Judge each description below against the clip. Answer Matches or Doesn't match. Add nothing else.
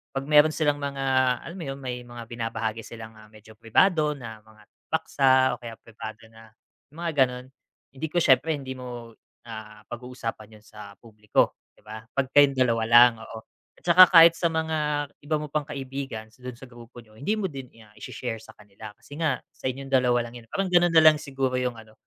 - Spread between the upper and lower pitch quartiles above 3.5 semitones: Matches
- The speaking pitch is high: Doesn't match